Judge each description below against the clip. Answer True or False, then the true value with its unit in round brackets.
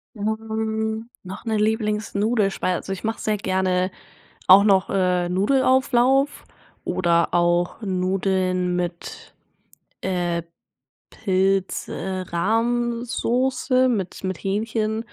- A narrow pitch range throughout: False (3.3 semitones)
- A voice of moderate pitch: False (200 Hz)